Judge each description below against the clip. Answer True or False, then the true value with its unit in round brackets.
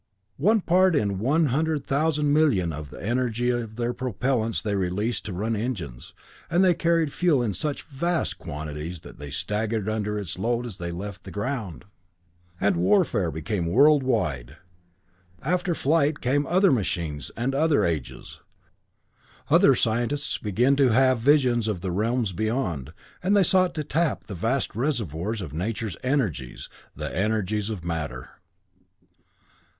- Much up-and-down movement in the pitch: True (7.2 semitones)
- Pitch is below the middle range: True (115 Hz)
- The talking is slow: False (155 wpm)